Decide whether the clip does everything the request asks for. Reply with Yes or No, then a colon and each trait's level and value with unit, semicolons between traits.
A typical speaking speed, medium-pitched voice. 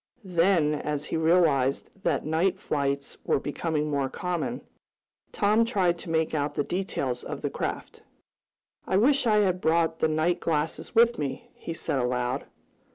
Yes: average, 160 wpm; medium, 160 Hz